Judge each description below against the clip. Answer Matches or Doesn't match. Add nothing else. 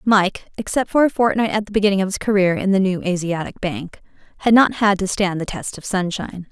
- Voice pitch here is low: Doesn't match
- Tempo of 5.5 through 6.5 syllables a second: Matches